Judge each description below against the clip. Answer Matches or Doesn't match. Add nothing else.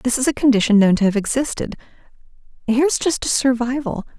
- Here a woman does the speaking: Matches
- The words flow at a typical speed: Matches